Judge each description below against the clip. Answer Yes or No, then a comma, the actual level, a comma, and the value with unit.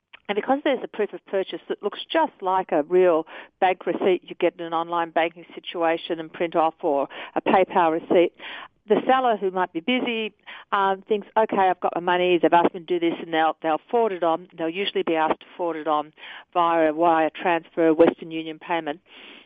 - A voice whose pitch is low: No, medium, 175 Hz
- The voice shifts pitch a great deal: No, average, 3.0 semitones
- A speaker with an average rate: No, fast, 215 wpm